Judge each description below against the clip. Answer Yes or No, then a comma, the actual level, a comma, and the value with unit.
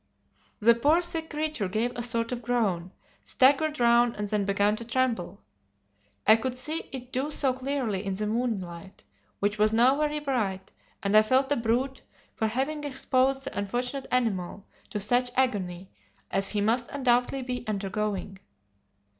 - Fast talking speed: No, average, 160 wpm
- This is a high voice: Yes, high, 235 Hz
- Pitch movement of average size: Yes, average, 4.2 semitones